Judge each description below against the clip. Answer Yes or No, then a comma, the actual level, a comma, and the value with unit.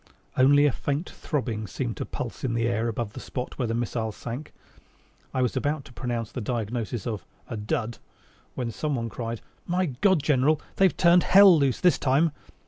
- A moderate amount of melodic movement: Yes, average, 4.1 semitones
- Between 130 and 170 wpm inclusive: No, average, 185 wpm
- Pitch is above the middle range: No, low, 125 Hz